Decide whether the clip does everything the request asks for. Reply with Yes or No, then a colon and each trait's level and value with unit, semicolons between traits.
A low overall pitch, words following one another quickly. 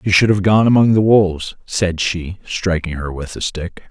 Yes: very low, 95 Hz; fast, 215 wpm